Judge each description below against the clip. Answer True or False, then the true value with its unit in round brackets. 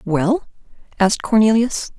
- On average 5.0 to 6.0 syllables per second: False (4.5 syllables/s)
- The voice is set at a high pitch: True (215 Hz)